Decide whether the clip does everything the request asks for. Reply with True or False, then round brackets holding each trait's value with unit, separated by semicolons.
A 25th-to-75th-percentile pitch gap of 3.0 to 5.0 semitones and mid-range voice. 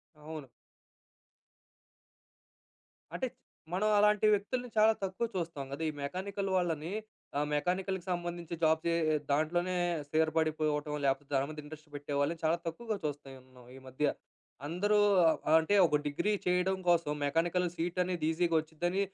True (3.5 semitones; 165 Hz)